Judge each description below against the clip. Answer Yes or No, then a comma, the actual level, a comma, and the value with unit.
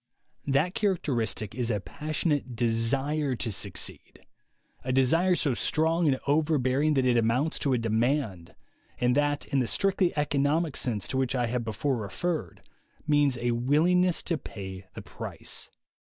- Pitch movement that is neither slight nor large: Yes, average, 4.6 semitones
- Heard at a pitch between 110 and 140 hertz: Yes, low, 135 Hz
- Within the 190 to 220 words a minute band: No, average, 150 wpm